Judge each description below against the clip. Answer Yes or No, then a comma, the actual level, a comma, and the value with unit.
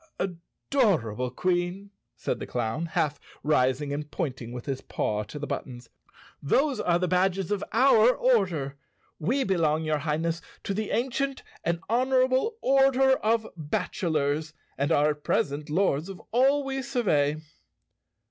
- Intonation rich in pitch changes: Yes, wide, 7.9 semitones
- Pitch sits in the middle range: Yes, medium, 170 Hz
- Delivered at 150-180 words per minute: No, average, 140 wpm